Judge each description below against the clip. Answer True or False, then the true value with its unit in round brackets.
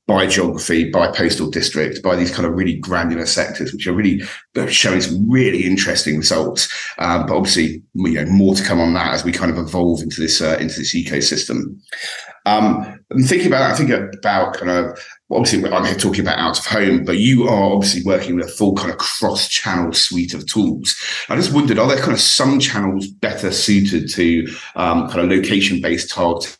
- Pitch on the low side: True (90 Hz)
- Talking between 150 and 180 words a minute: False (205 wpm)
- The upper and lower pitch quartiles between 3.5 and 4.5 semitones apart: False (2.7 semitones)